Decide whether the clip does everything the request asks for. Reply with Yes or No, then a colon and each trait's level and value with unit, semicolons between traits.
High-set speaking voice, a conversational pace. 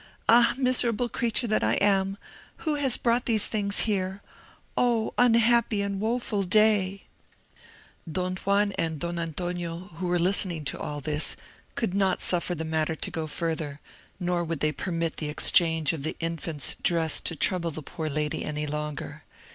No: medium, 180 Hz; average, 165 wpm